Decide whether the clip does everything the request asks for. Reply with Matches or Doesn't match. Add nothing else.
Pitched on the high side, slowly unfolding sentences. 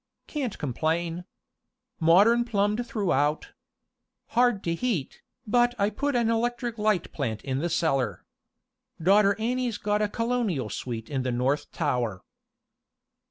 Matches